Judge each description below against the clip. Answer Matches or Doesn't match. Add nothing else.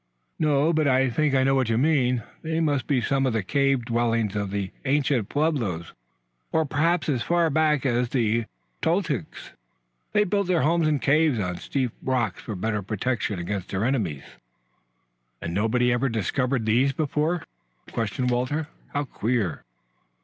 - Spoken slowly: Doesn't match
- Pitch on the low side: Matches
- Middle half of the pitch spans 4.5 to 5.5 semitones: Matches